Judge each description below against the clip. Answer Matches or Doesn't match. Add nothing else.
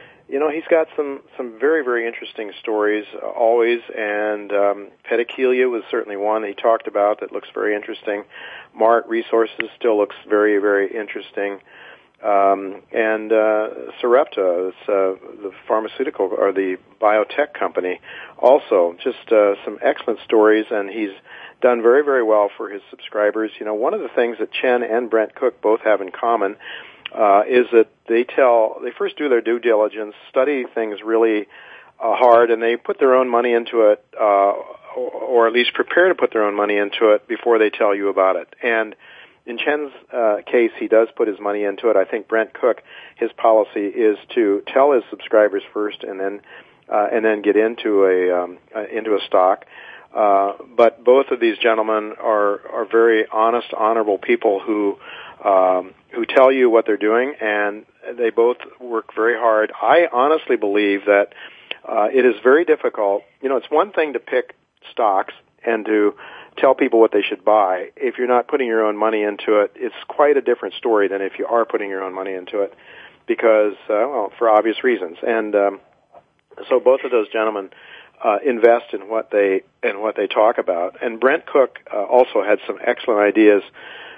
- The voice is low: Matches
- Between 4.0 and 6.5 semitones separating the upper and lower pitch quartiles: Doesn't match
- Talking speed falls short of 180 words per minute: Doesn't match